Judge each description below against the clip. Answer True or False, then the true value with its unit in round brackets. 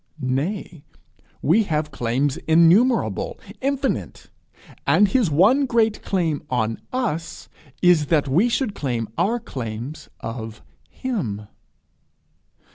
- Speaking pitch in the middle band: True (165 Hz)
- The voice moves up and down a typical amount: False (8.9 semitones)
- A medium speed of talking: False (105 wpm)